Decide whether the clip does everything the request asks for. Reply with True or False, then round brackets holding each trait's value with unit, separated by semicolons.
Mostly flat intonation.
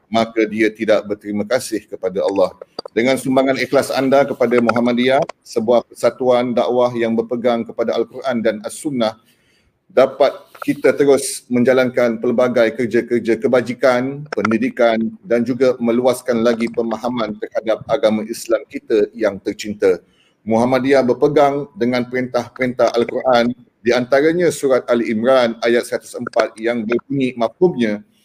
True (2.1 semitones)